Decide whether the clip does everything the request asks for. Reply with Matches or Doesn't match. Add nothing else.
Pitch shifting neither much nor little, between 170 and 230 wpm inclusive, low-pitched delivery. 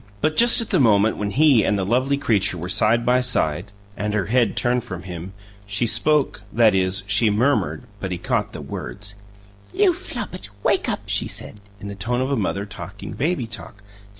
Matches